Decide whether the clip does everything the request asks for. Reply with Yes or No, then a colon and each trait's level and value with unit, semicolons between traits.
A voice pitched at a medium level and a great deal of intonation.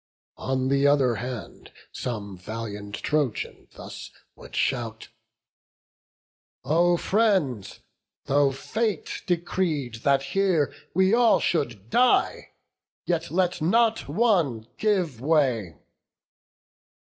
Yes: medium, 145 Hz; wide, 7.3 semitones